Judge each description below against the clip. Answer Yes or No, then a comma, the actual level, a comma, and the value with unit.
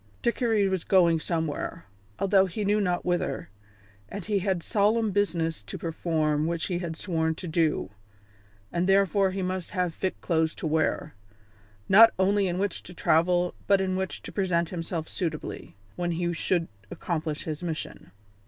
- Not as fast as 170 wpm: Yes, average, 160 wpm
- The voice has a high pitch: No, medium, 175 Hz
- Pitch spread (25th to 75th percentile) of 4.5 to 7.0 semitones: No, average, 2.8 semitones